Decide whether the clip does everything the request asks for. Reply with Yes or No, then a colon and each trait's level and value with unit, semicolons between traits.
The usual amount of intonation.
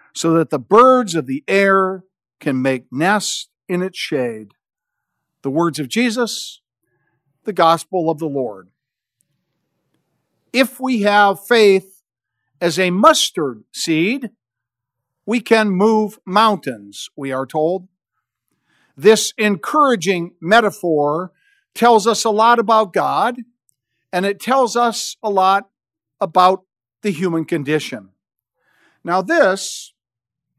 No: wide, 6.9 semitones